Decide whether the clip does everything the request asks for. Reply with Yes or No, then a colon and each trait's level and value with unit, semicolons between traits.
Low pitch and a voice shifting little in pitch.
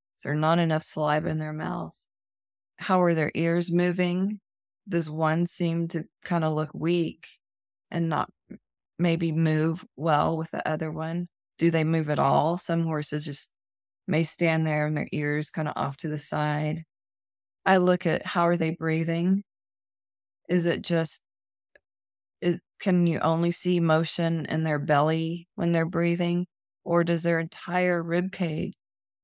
No: medium, 165 Hz; narrow, 2.2 semitones